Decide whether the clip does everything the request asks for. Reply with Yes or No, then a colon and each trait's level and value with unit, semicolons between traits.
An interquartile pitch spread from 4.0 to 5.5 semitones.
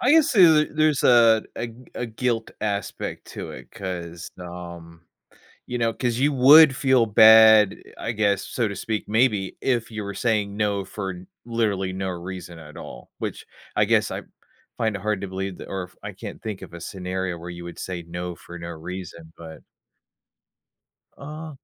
Yes: average, 4.7 semitones